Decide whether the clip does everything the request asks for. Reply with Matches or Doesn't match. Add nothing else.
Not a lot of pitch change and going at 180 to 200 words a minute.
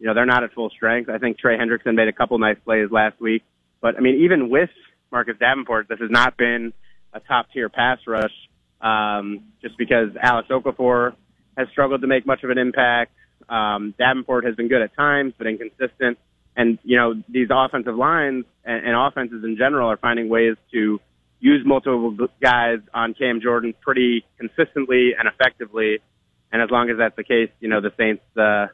Matches